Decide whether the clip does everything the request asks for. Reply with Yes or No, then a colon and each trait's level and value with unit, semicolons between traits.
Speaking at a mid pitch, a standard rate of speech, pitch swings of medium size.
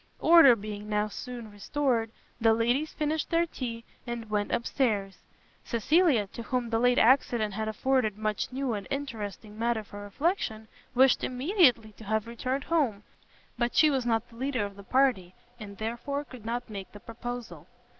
No: high, 235 Hz; average, 170 wpm; average, 3.7 semitones